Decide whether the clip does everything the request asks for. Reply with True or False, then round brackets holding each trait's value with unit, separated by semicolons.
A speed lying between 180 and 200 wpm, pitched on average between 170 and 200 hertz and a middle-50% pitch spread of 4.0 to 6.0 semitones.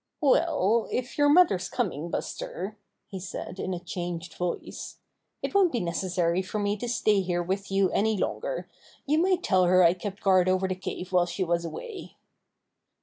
True (185 wpm; 190 Hz; 4.7 semitones)